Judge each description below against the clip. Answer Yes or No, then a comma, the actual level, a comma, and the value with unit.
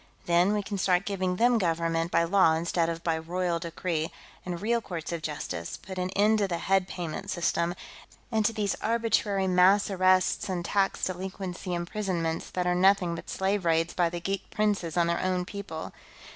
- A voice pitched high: No, medium, 180 Hz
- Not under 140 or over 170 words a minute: No, average, 185 wpm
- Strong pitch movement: No, average, 2.7 semitones